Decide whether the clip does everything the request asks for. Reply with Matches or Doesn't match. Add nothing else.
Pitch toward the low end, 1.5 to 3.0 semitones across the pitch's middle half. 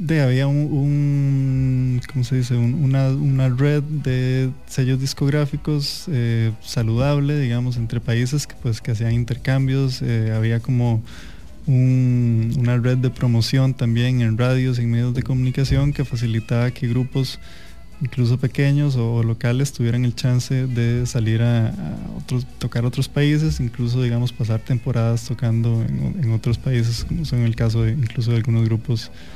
Matches